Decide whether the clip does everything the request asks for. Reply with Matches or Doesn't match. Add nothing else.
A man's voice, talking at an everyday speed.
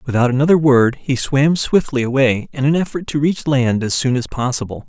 Doesn't match